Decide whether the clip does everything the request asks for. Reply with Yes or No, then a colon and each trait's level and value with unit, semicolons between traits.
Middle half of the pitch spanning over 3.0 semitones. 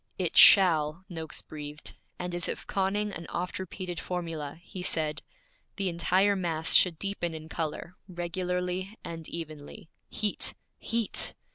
No: average, 2.7 semitones